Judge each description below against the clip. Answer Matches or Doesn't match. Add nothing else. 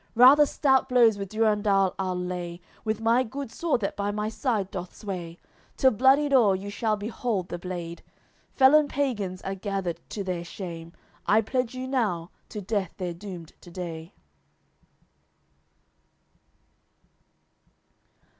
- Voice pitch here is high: Matches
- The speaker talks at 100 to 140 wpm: Matches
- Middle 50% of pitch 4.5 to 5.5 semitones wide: Matches